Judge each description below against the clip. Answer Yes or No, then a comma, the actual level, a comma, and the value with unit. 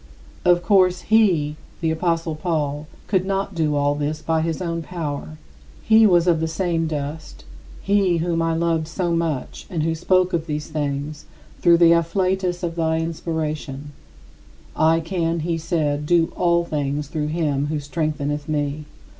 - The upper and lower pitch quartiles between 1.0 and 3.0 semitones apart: Yes, narrow, 2.4 semitones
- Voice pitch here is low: No, medium, 165 Hz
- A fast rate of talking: No, average, 165 wpm